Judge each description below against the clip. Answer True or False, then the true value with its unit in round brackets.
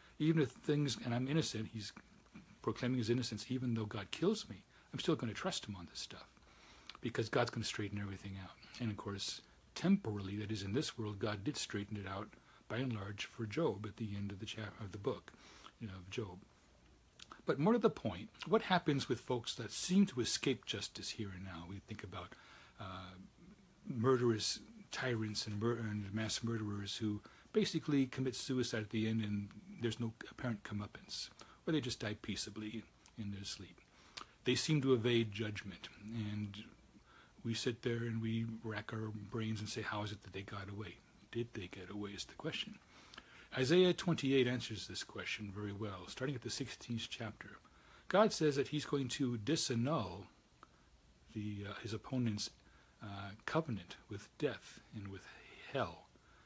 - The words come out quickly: False (180 wpm)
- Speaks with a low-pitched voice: True (110 Hz)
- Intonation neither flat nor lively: True (3.5 semitones)